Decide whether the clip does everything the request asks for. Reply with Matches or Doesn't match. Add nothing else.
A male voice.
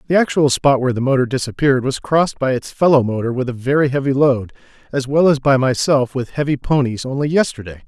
Matches